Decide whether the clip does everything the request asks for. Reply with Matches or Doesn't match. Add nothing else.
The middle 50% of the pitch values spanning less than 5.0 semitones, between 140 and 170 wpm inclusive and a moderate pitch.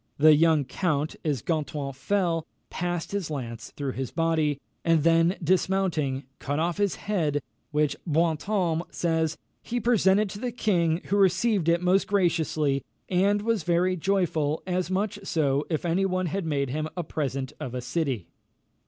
Matches